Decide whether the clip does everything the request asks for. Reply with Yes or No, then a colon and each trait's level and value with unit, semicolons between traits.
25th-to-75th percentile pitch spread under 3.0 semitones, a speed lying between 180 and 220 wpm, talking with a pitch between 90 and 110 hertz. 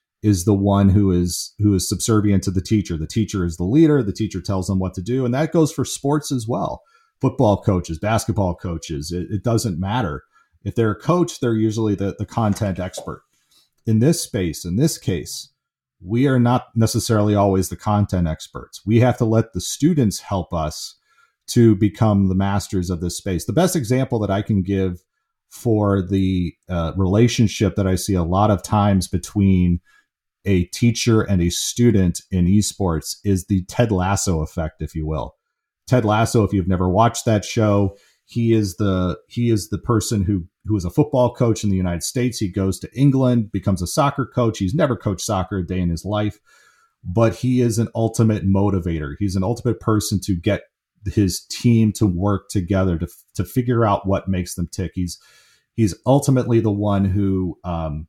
No: average, 3.8 semitones; average, 190 wpm; low, 105 Hz